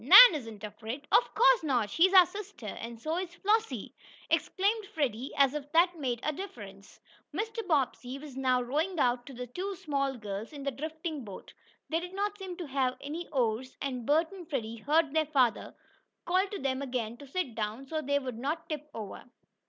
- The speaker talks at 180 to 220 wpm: Yes, average, 195 wpm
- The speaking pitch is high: Yes, very high, 285 Hz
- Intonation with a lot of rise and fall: Yes, wide, 5.8 semitones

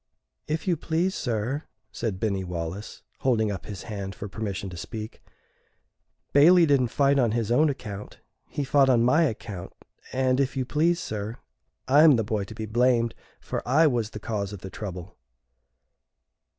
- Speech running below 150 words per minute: No, average, 170 wpm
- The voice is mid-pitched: No, low, 115 Hz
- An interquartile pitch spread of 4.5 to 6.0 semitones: Yes, average, 5.2 semitones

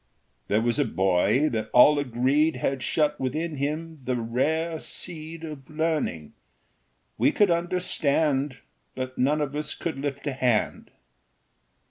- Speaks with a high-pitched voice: No, medium, 145 Hz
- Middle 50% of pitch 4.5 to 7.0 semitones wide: No, average, 3.7 semitones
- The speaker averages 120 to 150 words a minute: Yes, slow, 135 wpm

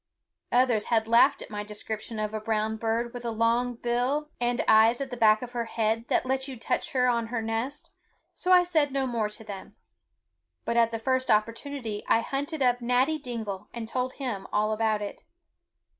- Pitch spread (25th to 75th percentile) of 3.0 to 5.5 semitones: No, narrow, 2.6 semitones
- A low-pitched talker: No, high, 235 Hz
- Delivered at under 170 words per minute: No, average, 200 wpm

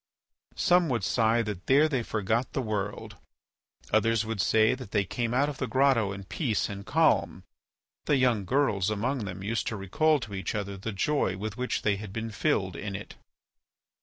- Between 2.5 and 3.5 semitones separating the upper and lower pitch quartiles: No, average, 4.4 semitones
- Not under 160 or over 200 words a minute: Yes, average, 190 wpm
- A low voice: Yes, low, 110 Hz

